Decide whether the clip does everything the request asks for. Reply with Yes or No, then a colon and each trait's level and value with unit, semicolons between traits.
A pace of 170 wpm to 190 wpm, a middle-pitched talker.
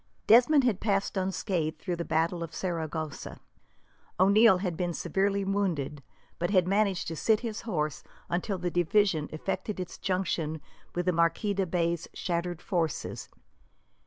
No: average, 145 wpm; medium, 180 Hz